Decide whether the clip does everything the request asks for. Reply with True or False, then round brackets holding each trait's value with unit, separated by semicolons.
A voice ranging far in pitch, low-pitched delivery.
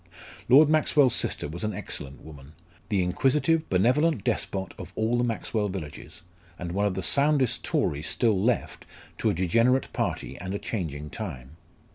True (6.5 semitones; 100 Hz)